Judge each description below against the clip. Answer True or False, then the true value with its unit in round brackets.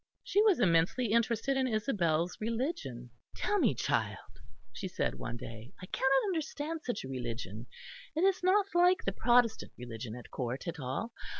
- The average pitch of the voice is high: True (220 Hz)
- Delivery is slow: False (165 wpm)